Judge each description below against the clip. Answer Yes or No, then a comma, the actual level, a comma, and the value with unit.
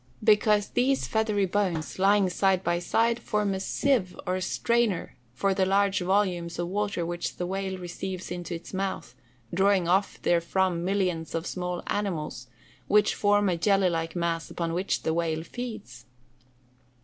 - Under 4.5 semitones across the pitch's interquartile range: Yes, average, 2.8 semitones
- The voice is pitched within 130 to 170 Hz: No, high, 190 Hz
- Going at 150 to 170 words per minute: Yes, average, 160 wpm